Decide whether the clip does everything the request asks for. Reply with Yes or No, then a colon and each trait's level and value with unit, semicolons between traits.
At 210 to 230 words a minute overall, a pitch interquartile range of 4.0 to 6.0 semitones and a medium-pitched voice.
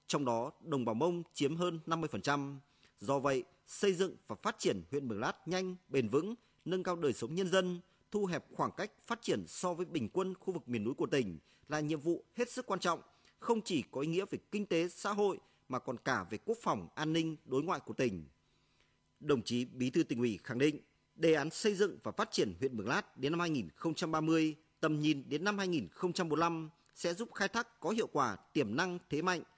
Yes: average, 220 wpm; average, 4.8 semitones; medium, 165 Hz